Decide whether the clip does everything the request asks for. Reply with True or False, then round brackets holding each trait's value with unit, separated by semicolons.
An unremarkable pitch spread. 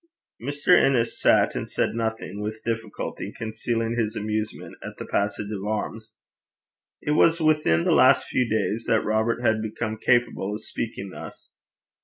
False (1.9 semitones)